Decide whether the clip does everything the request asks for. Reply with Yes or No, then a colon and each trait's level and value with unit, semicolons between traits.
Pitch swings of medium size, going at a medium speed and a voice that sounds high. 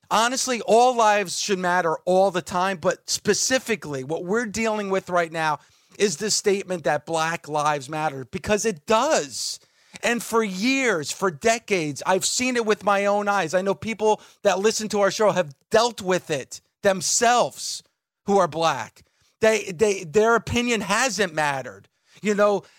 Yes: average, 3.6 semitones; average, 165 wpm; high, 200 Hz